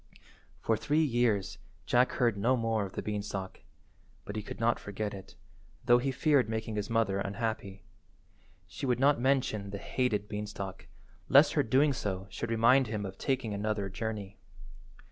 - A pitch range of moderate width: Yes, average, 3.2 semitones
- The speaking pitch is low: Yes, low, 110 Hz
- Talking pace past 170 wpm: No, average, 165 wpm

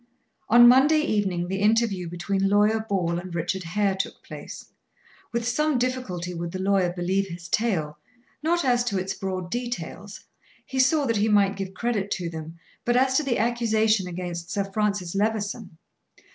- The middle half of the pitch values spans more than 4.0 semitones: Yes, average, 4.6 semitones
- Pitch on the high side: Yes, high, 200 Hz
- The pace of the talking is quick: No, average, 170 wpm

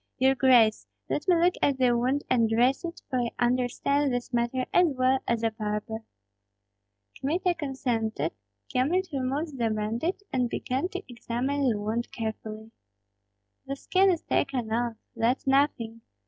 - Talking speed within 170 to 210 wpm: No, average, 150 wpm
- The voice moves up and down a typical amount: Yes, average, 3.5 semitones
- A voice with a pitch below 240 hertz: No, very high, 255 Hz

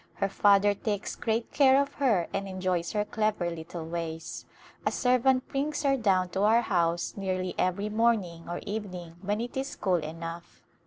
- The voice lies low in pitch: No, high, 200 Hz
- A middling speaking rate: Yes, average, 170 wpm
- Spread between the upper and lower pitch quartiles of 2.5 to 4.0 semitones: No, average, 4.6 semitones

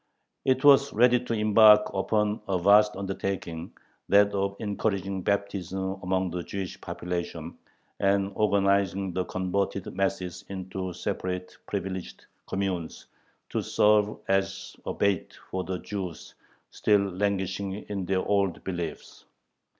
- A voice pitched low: Yes, very low, 95 Hz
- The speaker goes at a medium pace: No, slow, 120 wpm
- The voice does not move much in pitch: Yes, narrow, 1.6 semitones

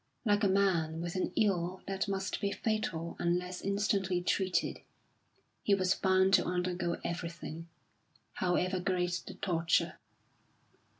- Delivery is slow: Yes, slow, 125 wpm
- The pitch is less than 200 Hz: Yes, medium, 185 Hz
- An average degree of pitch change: No, narrow, 2.0 semitones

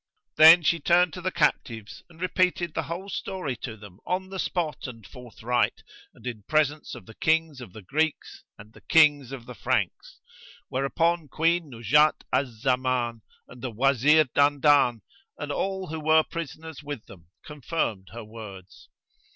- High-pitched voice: No, medium, 145 Hz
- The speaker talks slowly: No, average, 160 wpm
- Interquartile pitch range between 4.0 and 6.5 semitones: Yes, wide, 5.4 semitones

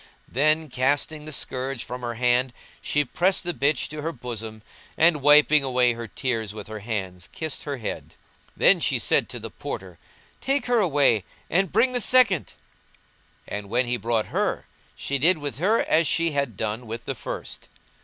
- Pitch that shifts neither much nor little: Yes, average, 5.0 semitones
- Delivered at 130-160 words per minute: No, average, 180 wpm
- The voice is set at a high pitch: No, low, 135 Hz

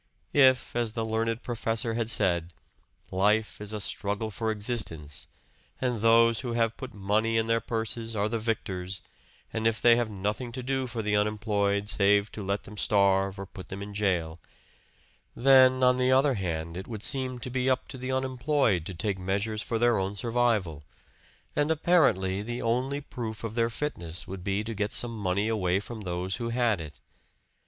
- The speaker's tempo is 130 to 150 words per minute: No, average, 185 wpm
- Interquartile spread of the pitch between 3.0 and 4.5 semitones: Yes, average, 3.3 semitones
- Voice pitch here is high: No, low, 110 Hz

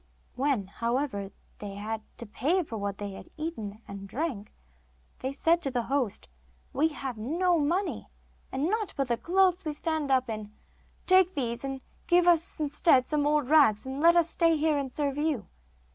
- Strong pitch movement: Yes, wide, 5.9 semitones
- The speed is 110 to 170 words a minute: No, average, 180 wpm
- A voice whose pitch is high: Yes, very high, 280 Hz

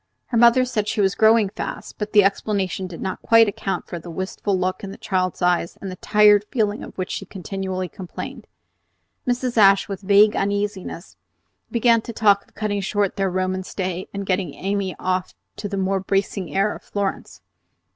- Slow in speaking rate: No, average, 185 wpm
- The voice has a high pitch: Yes, high, 195 Hz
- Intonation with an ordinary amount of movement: No, narrow, 1.9 semitones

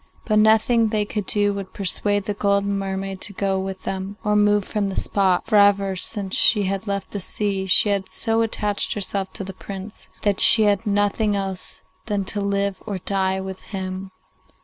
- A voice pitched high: Yes, high, 200 Hz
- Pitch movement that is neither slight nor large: No, narrow, 1.3 semitones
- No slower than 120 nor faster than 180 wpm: No, average, 195 wpm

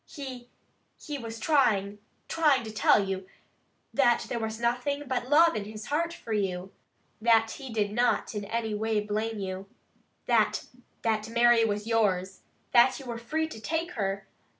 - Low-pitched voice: No, high, 225 Hz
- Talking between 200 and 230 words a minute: No, average, 165 wpm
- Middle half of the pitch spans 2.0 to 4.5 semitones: Yes, average, 3.4 semitones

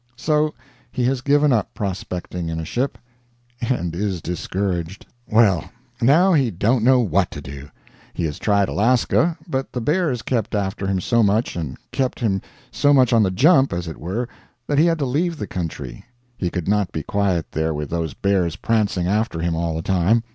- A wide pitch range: Yes, wide, 6.6 semitones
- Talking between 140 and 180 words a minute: No, average, 190 wpm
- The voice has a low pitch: Yes, low, 100 Hz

